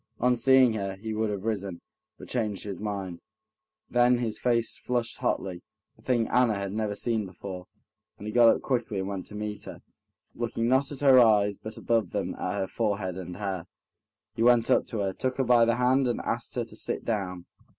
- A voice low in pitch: Yes, low, 110 Hz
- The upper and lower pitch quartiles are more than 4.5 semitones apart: No, average, 3.5 semitones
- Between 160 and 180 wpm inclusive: No, fast, 205 wpm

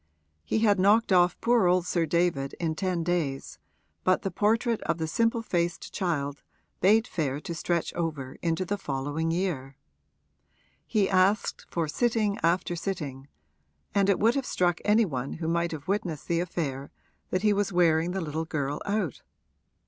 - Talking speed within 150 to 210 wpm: Yes, average, 165 wpm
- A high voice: No, medium, 175 Hz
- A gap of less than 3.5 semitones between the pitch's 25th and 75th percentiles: No, average, 3.9 semitones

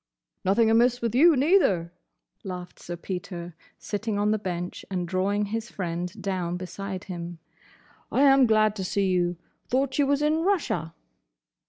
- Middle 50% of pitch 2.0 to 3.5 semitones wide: No, average, 5.2 semitones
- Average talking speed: Yes, average, 155 wpm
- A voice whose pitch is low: No, high, 200 Hz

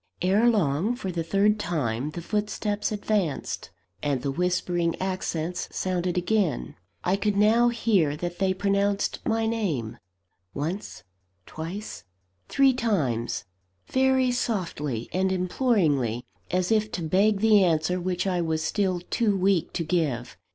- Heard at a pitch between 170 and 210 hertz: Yes, medium, 185 Hz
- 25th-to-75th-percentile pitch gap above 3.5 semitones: Yes, average, 4.6 semitones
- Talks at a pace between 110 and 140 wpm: Yes, slow, 135 wpm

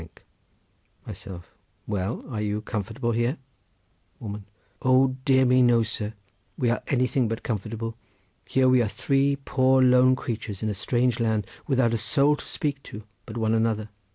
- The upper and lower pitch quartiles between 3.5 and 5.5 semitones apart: No, average, 3.1 semitones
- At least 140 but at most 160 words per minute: Yes, average, 150 wpm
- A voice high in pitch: No, low, 115 Hz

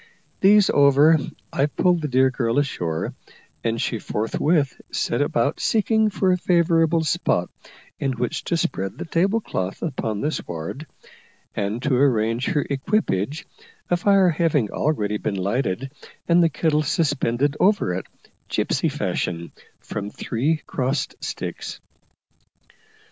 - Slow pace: Yes, slow, 130 wpm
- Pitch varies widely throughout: Yes, wide, 6.7 semitones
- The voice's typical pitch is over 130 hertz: Yes, medium, 140 Hz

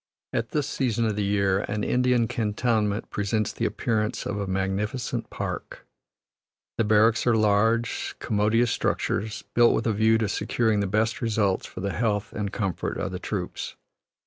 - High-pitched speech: No, low, 110 Hz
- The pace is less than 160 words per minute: No, average, 165 wpm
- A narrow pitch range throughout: Yes, narrow, 1.9 semitones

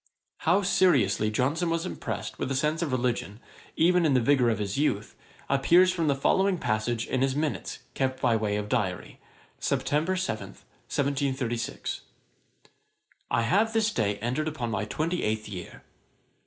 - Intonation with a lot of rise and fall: Yes, wide, 6.7 semitones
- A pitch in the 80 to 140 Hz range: Yes, low, 135 Hz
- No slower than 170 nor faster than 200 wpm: No, average, 160 wpm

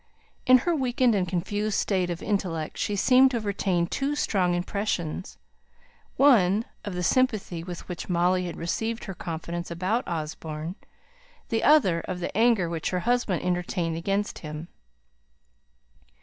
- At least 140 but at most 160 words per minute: Yes, average, 150 wpm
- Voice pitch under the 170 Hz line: No, medium, 185 Hz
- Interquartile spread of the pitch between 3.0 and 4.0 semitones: No, average, 4.5 semitones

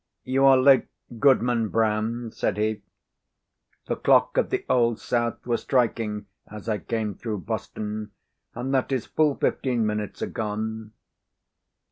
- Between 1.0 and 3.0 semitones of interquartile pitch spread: Yes, average, 2.7 semitones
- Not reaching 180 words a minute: Yes, slow, 135 wpm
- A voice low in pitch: Yes, low, 115 Hz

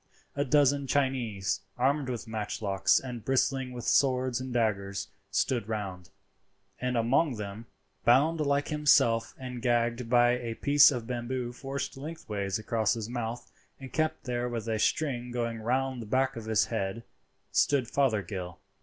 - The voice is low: Yes, low, 120 Hz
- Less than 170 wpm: Yes, average, 150 wpm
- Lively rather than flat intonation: No, average, 3.1 semitones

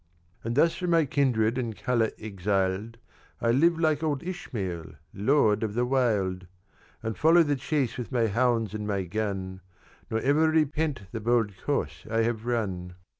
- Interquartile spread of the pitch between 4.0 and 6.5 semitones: Yes, average, 5.2 semitones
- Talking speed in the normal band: Yes, average, 165 wpm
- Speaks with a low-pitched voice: Yes, low, 115 Hz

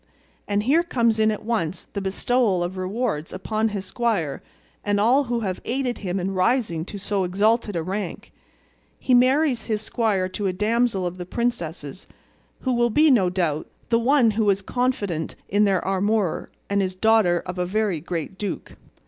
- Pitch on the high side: Yes, high, 205 Hz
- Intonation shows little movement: No, average, 4.2 semitones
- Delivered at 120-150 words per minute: No, average, 180 wpm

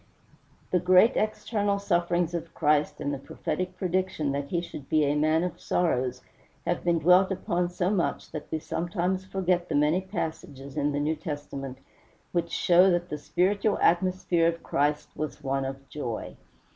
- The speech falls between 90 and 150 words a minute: No, average, 170 wpm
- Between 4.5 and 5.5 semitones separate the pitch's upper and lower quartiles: No, average, 3.7 semitones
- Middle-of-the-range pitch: Yes, medium, 170 Hz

